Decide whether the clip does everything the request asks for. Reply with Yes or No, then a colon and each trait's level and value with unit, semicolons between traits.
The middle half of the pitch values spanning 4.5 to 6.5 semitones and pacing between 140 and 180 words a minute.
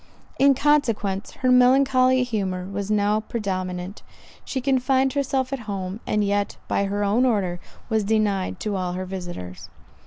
Yes: average, 4.9 semitones; average, 150 wpm